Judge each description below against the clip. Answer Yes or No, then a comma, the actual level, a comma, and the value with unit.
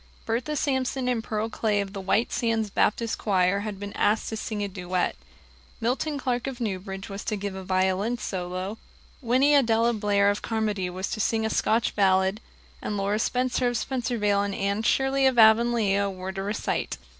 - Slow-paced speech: No, average, 180 wpm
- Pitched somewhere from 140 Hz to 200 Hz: No, high, 215 Hz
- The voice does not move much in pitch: No, average, 3.2 semitones